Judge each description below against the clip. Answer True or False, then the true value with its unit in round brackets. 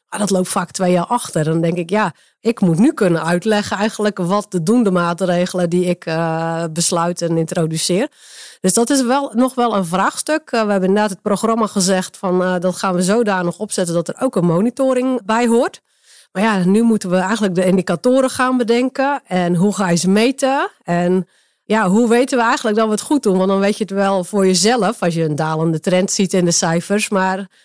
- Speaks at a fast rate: True (220 wpm)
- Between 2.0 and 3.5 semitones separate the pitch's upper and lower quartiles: False (4.2 semitones)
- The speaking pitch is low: False (195 Hz)